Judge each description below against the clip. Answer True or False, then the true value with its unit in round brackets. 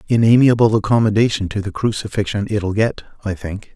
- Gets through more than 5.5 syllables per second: True (5.8 syllables/s)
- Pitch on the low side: True (105 Hz)